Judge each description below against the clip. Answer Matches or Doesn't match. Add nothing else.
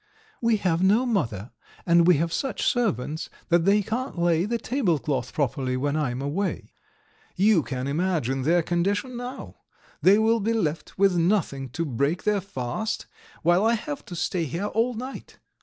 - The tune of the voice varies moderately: Doesn't match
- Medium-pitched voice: Matches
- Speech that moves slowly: Doesn't match